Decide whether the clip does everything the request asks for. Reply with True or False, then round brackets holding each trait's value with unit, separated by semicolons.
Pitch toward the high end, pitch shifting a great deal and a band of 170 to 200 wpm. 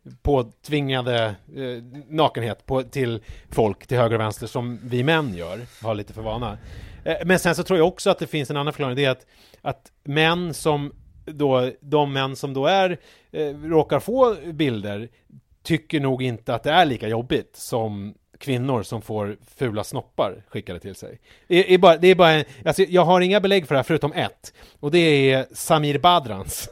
False (135 Hz; 5.7 semitones; 190 wpm)